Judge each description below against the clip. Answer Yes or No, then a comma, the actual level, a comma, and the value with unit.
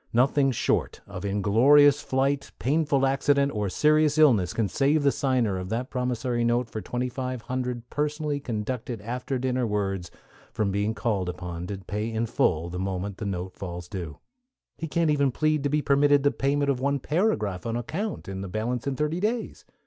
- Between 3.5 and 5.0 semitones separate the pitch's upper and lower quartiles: No, wide, 5.5 semitones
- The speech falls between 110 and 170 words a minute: No, average, 185 wpm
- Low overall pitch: Yes, low, 125 Hz